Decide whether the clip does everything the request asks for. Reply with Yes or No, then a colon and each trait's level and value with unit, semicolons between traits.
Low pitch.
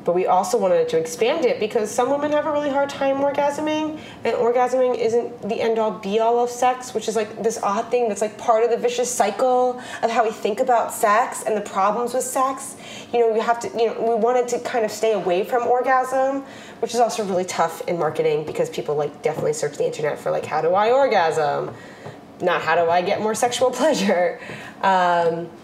No: high, 240 Hz